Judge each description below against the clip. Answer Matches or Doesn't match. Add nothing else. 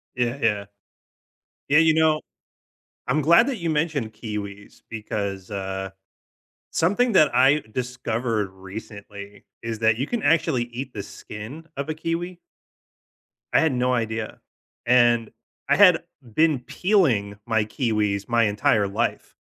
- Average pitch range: Doesn't match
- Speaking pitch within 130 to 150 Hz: Doesn't match